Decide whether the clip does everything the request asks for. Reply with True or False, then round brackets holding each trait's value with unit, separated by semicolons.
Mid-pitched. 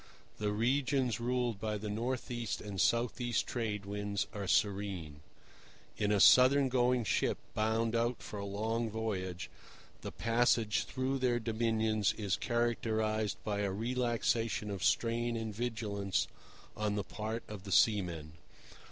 False (110 Hz)